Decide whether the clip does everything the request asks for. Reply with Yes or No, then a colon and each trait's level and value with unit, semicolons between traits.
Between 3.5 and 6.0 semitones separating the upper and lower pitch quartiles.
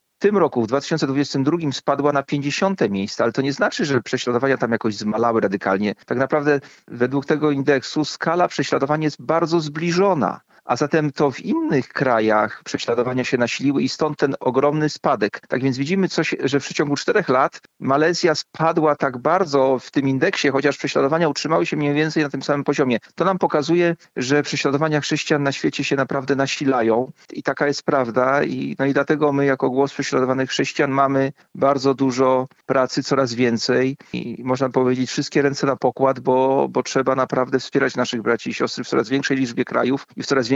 No: narrow, 2.5 semitones